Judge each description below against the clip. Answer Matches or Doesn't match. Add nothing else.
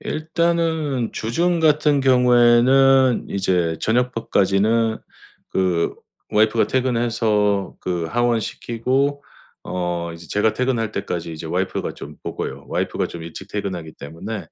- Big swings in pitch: Matches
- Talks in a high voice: Doesn't match